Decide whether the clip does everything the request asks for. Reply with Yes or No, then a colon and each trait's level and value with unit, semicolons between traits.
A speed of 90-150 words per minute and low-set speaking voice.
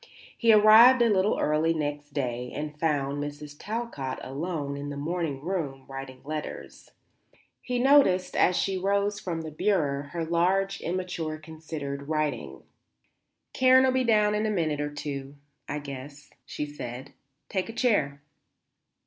No: average, 145 wpm; medium, 155 Hz